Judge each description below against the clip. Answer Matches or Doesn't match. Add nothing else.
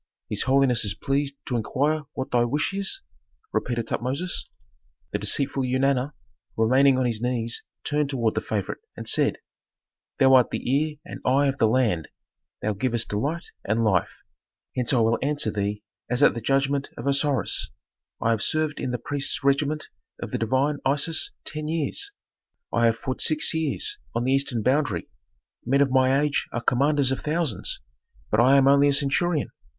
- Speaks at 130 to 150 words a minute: Doesn't match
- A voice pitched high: Doesn't match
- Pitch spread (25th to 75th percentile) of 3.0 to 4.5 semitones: Matches